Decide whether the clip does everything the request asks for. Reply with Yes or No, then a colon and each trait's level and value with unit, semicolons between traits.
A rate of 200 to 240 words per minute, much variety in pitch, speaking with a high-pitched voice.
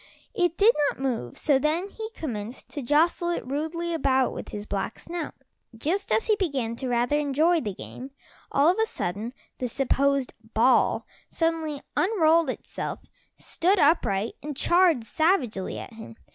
No: average, 160 wpm; wide, 5.8 semitones; very high, 290 Hz